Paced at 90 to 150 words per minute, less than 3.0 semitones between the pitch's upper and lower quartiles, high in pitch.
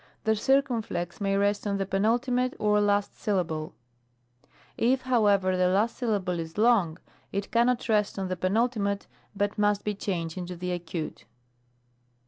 No: average, 145 wpm; average, 3.3 semitones; high, 205 Hz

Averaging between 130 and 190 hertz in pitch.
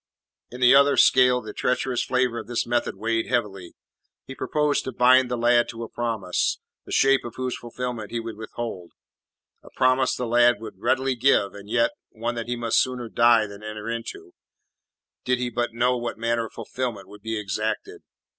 No: low, 120 Hz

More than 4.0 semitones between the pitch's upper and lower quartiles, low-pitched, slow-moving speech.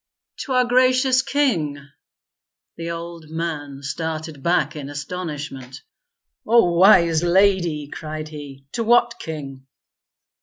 No: average, 4.8 semitones; medium, 165 Hz; slow, 110 wpm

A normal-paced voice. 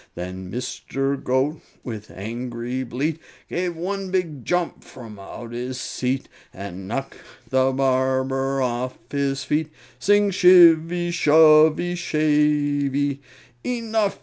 No: slow, 110 wpm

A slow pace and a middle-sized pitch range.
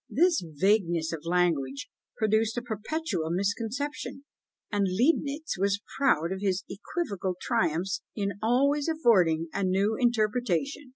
No: slow, 120 wpm; wide, 5.7 semitones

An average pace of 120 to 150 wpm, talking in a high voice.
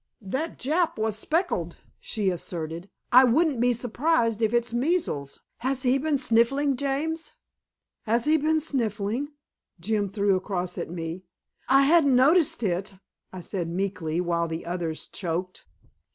Yes: average, 140 wpm; high, 230 Hz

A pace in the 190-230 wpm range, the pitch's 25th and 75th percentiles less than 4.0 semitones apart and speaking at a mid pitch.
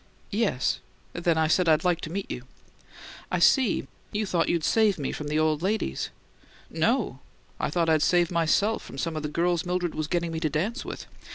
Yes: average, 200 wpm; average, 2.8 semitones; medium, 170 Hz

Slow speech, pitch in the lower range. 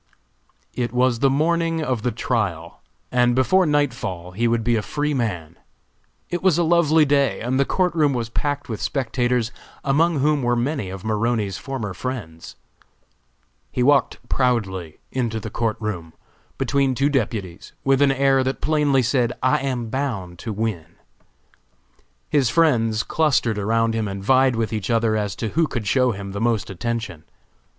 No: average, 165 wpm; low, 120 Hz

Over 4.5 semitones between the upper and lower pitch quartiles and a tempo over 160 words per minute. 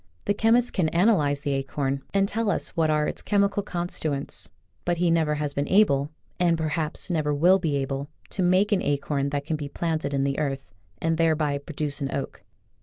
No: average, 3.8 semitones; average, 195 wpm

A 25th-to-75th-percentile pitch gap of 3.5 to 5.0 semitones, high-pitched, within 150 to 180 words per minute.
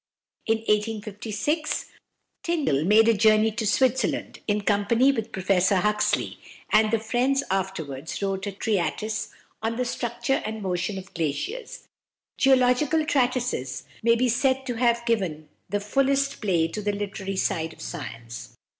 No: average, 4.2 semitones; high, 215 Hz; average, 140 wpm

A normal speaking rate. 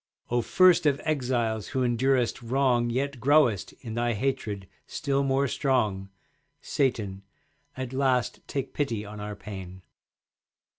No: slow, 130 wpm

